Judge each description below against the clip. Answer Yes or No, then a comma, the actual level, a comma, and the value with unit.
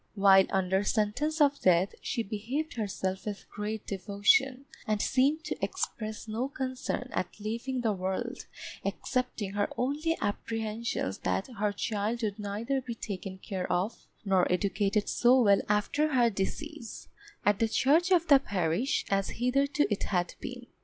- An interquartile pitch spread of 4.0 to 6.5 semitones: Yes, average, 4.5 semitones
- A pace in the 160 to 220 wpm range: No, average, 150 wpm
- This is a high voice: Yes, high, 215 Hz